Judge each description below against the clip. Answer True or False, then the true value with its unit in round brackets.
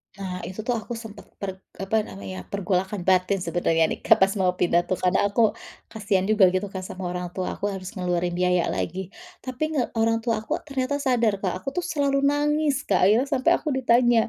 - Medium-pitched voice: False (200 Hz)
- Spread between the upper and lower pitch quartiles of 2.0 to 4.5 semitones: False (4.9 semitones)